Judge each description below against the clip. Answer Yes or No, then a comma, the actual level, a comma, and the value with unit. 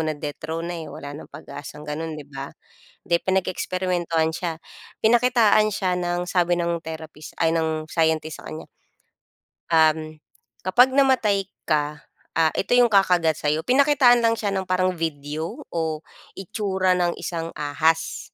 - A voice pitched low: No, medium, 170 Hz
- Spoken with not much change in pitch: No, average, 3.3 semitones